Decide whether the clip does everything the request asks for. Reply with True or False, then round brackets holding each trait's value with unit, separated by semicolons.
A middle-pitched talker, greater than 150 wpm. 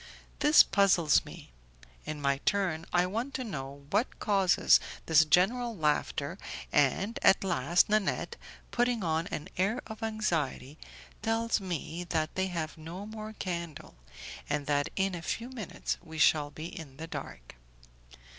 False (175 Hz; 145 wpm)